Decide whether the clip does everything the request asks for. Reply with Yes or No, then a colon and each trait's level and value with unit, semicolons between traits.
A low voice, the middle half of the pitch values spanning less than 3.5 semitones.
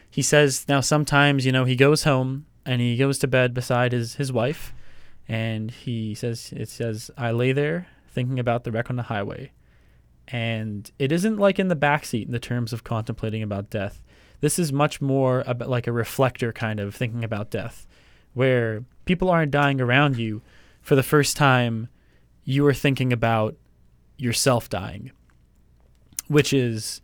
No: low, 125 Hz; average, 3.8 semitones